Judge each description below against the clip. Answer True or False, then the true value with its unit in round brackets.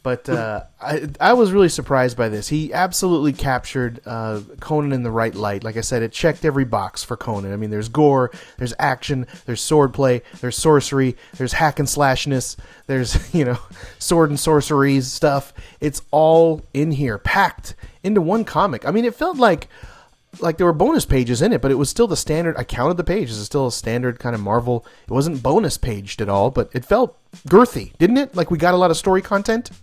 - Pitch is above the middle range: False (135 Hz)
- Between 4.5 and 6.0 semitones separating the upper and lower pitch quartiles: True (5.3 semitones)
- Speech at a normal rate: False (210 wpm)